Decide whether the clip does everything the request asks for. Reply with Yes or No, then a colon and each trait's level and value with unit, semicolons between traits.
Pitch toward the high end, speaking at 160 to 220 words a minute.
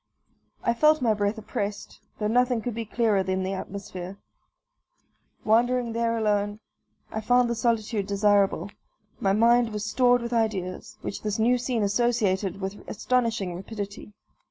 No: high, 215 Hz; average, 145 wpm